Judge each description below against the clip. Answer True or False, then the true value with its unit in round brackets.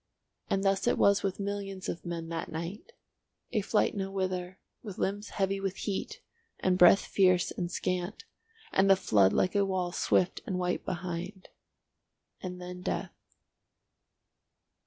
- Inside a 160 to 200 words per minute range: False (140 wpm)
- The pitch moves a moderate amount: False (1.6 semitones)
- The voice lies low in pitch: False (185 Hz)